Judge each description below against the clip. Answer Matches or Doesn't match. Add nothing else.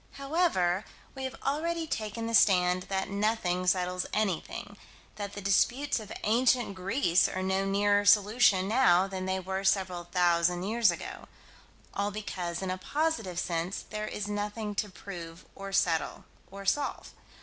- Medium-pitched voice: Doesn't match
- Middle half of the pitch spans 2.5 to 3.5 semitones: Matches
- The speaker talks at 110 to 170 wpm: Matches